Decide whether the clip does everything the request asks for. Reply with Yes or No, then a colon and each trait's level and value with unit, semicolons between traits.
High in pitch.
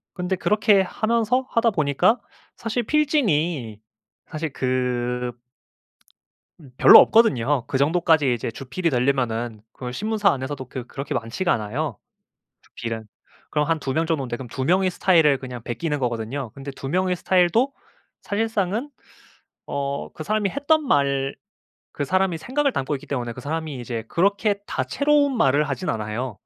No: medium, 150 Hz